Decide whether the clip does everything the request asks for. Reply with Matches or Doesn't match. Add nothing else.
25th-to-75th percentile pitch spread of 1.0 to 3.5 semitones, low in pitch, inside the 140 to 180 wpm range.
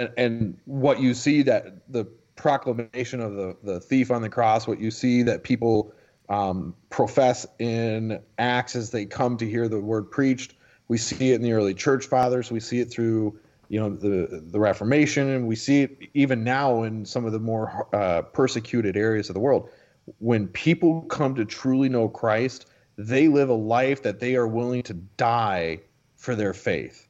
Doesn't match